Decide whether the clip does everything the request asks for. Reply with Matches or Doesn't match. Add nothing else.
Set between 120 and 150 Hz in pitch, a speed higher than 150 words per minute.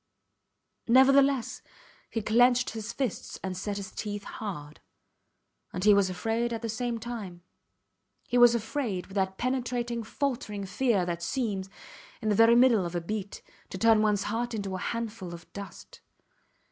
Doesn't match